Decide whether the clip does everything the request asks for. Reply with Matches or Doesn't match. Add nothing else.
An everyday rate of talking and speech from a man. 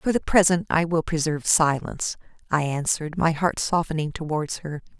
Doesn't match